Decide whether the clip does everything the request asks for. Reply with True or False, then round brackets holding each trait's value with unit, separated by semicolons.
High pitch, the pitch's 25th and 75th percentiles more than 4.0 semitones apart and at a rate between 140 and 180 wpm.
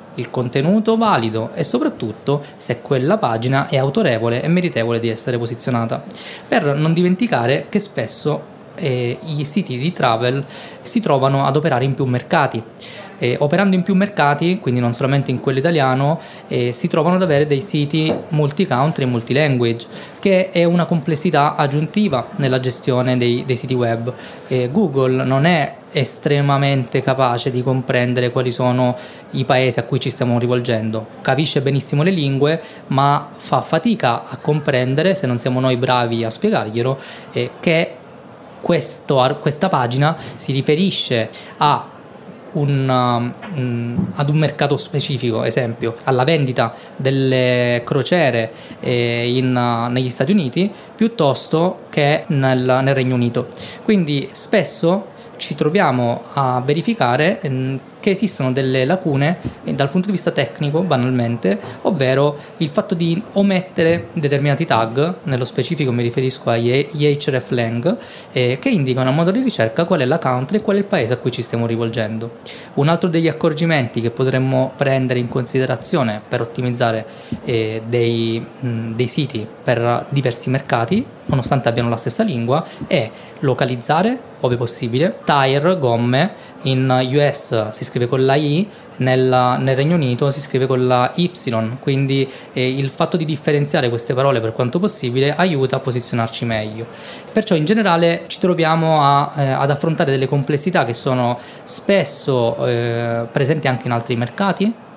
False (135 Hz; 4.7 semitones; 150 wpm)